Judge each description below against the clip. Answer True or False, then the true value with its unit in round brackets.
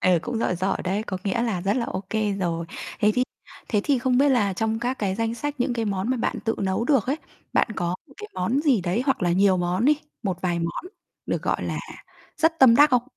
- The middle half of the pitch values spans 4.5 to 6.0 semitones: True (5.4 semitones)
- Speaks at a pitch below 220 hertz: False (225 Hz)